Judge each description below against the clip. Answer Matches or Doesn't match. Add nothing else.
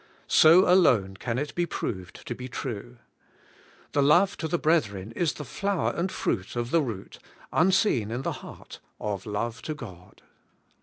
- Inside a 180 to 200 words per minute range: Doesn't match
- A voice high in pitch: Doesn't match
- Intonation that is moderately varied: Doesn't match